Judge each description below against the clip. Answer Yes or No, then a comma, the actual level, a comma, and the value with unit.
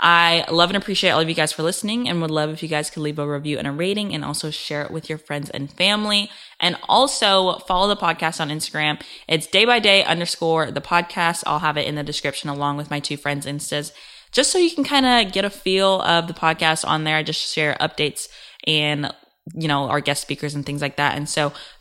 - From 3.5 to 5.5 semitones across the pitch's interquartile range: Yes, average, 3.8 semitones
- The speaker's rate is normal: No, fast, 240 wpm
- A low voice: No, medium, 160 Hz